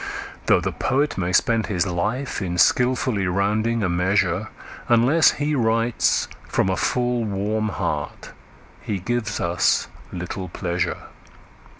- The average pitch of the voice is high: No, low, 110 Hz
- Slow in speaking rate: Yes, slow, 125 wpm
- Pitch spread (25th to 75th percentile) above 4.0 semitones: Yes, average, 4.7 semitones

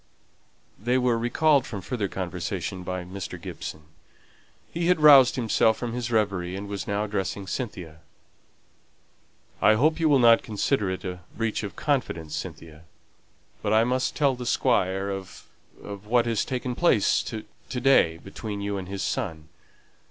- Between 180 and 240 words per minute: No, average, 155 wpm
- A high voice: No, low, 105 Hz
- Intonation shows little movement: No, average, 4.6 semitones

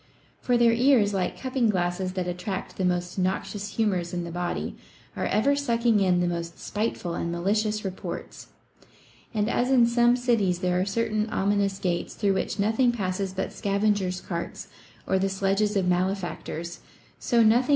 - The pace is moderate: Yes, average, 170 wpm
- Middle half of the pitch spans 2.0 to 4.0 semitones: Yes, average, 3.7 semitones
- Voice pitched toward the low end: No, high, 195 Hz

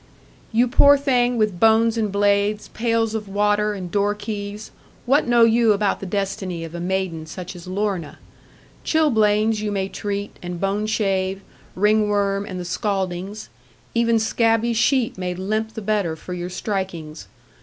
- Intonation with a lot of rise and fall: No, average, 2.7 semitones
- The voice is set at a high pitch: Yes, high, 205 Hz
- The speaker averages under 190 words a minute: Yes, average, 155 wpm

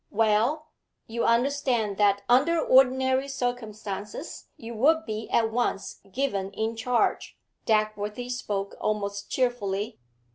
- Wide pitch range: No, average, 3.5 semitones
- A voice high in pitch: Yes, high, 225 Hz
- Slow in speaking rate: Yes, slow, 110 wpm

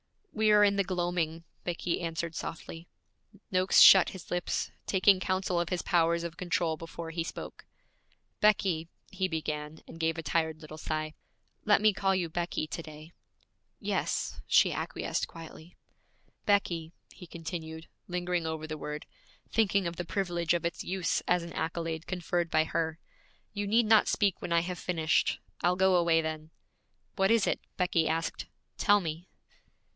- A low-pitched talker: No, medium, 170 Hz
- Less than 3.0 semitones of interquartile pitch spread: Yes, narrow, 2.5 semitones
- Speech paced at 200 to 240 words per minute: No, average, 160 wpm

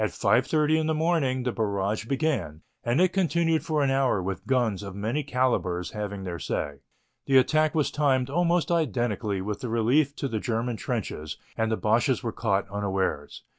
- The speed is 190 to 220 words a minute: No, average, 175 wpm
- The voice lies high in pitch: No, low, 120 Hz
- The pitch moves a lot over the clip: Yes, wide, 6.4 semitones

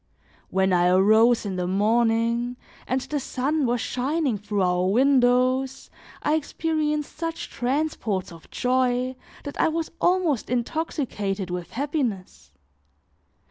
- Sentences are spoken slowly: Yes, slow, 120 wpm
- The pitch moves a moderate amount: No, wide, 6.0 semitones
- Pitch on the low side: No, high, 245 Hz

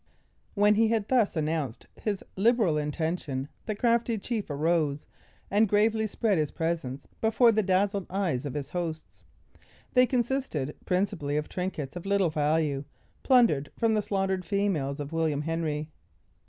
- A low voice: No, medium, 180 Hz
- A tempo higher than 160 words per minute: No, average, 145 wpm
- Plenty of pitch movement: Yes, wide, 5.9 semitones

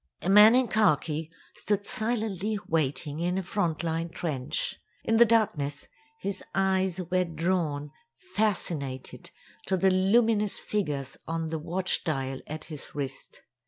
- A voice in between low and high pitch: Yes, medium, 180 Hz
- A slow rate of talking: Yes, slow, 130 wpm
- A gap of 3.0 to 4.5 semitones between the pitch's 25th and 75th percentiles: No, average, 4.9 semitones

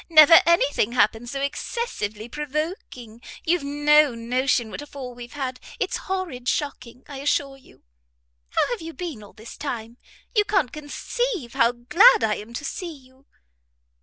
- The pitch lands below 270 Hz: No, very high, 275 Hz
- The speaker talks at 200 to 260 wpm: No, average, 165 wpm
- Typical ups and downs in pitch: Yes, average, 4.7 semitones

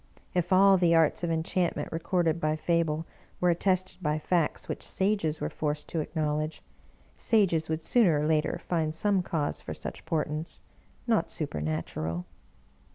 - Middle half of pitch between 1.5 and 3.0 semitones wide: Yes, narrow, 2.6 semitones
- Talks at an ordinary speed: Yes, average, 160 wpm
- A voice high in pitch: No, medium, 160 Hz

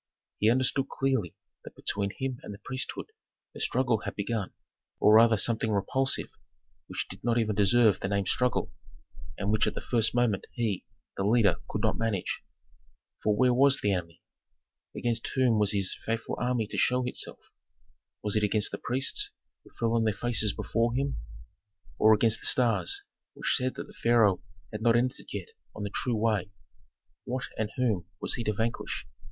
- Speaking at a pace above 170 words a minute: Yes, average, 180 wpm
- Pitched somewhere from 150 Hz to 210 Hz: No, low, 115 Hz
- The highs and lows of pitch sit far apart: No, average, 2.9 semitones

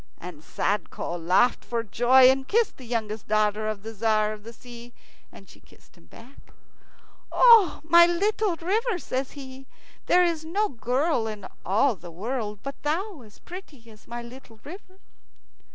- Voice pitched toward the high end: Yes, high, 245 Hz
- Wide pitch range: Yes, wide, 7.4 semitones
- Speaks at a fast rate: No, average, 165 wpm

